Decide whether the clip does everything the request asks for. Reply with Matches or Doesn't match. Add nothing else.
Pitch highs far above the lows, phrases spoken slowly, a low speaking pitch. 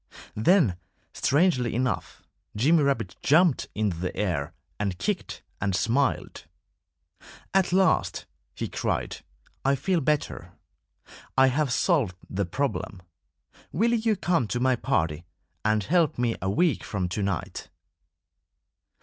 Matches